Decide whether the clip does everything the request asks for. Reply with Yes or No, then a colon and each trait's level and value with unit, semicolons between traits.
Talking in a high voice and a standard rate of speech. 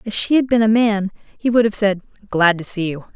No: high, 210 Hz; fast, 265 wpm